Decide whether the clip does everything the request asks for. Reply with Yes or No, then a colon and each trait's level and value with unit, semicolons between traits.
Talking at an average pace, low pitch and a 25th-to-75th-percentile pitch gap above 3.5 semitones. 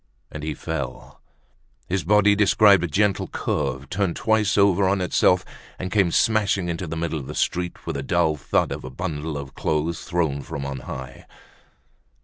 Yes: average, 175 wpm; very low, 85 Hz; average, 4.9 semitones